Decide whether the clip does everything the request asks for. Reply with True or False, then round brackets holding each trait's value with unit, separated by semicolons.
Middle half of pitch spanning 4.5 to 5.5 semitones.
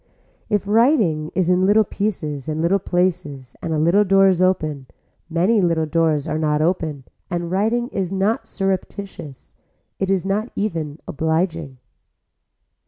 False (3.9 semitones)